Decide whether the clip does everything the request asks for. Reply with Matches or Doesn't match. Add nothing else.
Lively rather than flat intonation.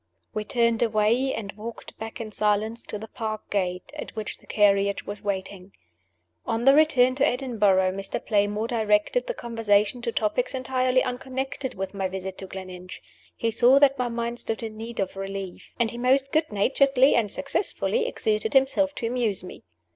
Doesn't match